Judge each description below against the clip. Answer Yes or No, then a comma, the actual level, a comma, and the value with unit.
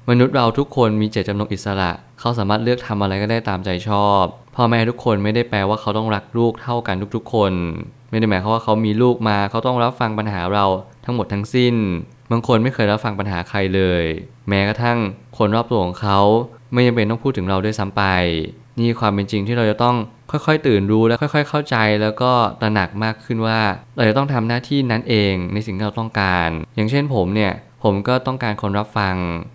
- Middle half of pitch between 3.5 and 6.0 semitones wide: No, average, 3.0 semitones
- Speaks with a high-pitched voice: No, low, 110 Hz